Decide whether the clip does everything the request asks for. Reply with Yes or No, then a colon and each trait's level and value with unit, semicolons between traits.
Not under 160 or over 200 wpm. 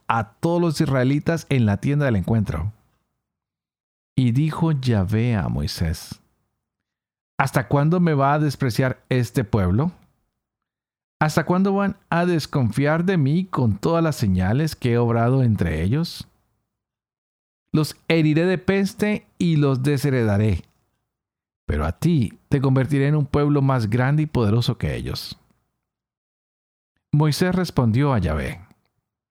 No: average, 130 wpm